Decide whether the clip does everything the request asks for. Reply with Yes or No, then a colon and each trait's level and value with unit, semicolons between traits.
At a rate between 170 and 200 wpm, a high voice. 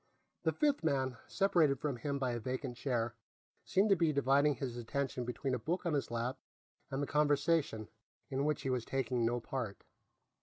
No: average, 185 wpm; low, 135 Hz